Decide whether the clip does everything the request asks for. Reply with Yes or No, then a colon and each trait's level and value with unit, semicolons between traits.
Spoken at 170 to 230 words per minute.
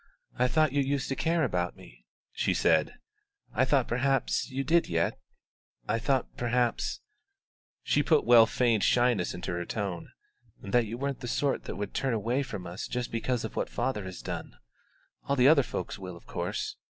Yes: average, 185 wpm